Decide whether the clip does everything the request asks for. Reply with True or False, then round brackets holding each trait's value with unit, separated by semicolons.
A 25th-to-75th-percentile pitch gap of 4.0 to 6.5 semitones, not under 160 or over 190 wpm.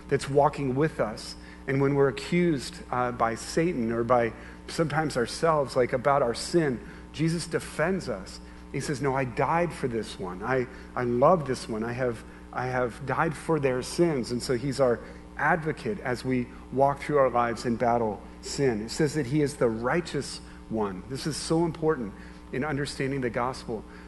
True (4.6 semitones; 180 wpm)